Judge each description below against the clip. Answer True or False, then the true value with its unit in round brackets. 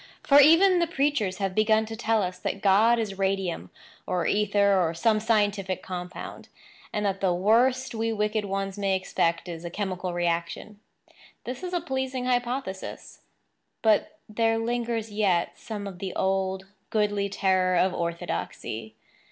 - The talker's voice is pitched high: True (205 Hz)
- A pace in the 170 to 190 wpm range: False (150 wpm)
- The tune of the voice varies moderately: True (3.3 semitones)